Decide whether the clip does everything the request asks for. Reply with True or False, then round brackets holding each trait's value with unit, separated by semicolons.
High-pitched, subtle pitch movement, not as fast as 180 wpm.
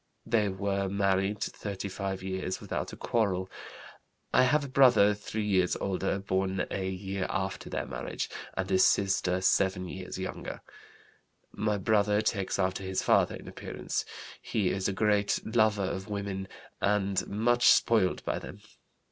False (100 Hz; 1.7 semitones; 150 wpm)